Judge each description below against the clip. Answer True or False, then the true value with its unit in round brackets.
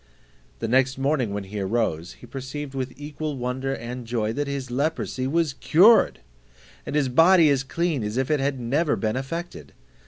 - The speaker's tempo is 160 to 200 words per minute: True (180 wpm)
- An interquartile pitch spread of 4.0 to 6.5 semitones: False (3.4 semitones)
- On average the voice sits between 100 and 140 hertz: True (135 Hz)